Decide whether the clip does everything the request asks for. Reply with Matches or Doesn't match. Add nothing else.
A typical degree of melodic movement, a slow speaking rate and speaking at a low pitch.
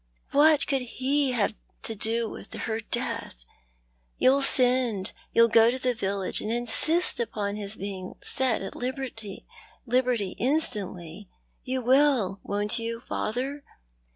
Doesn't match